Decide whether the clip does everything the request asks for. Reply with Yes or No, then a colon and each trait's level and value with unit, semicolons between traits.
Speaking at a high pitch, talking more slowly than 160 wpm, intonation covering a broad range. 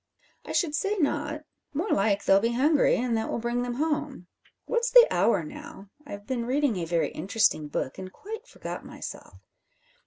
No: high, 245 Hz; average, 180 wpm; wide, 7.0 semitones